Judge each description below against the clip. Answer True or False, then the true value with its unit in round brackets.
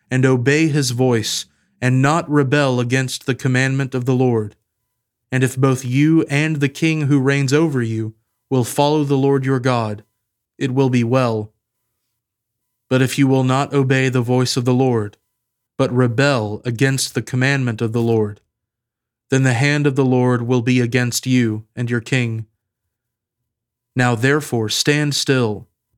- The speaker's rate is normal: True (160 wpm)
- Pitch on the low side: True (125 Hz)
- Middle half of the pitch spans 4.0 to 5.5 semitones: False (2.6 semitones)